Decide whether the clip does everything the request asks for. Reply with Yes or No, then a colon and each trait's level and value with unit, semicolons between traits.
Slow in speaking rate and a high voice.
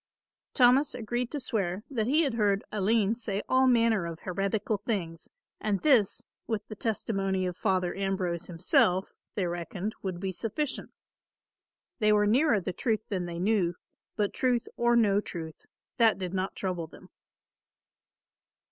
No: average, 150 wpm; high, 205 Hz